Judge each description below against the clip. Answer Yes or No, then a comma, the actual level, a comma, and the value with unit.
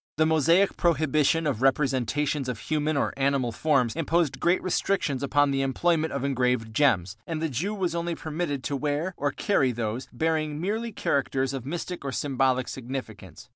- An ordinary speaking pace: Yes, average, 170 wpm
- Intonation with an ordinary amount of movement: Yes, average, 3.7 semitones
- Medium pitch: Yes, medium, 145 Hz